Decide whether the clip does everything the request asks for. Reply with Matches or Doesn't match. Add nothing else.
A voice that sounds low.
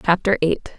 Doesn't match